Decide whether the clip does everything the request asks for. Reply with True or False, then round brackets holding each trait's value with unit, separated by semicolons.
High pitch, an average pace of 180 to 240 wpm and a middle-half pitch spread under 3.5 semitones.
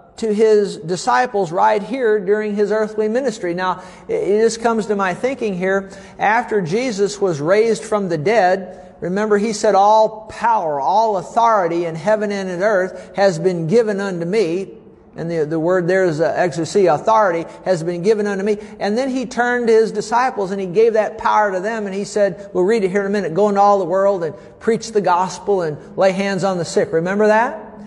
True (205 Hz; 205 wpm; 2.8 semitones)